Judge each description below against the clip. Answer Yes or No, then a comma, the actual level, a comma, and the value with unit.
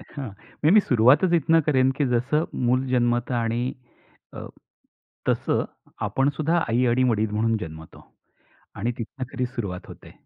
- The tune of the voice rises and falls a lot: No, average, 3.6 semitones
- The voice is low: Yes, low, 125 Hz